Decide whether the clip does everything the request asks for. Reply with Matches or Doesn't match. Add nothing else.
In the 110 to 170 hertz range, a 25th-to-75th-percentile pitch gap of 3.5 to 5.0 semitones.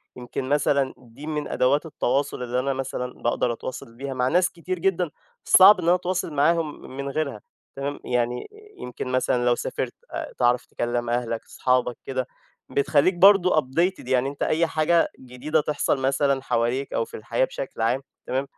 Matches